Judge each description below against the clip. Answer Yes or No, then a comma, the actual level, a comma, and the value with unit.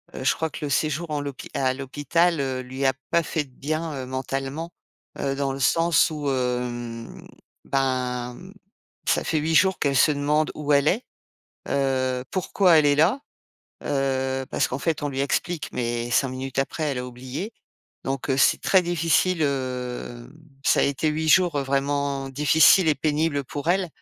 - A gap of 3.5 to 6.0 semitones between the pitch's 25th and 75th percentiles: No, average, 3.1 semitones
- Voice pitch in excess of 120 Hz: Yes, medium, 140 Hz